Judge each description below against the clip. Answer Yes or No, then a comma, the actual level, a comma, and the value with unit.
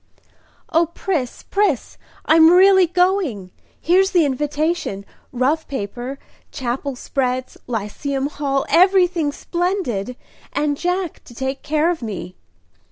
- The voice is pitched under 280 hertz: No, very high, 295 Hz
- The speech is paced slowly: Yes, slow, 110 wpm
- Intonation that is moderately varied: No, wide, 5.8 semitones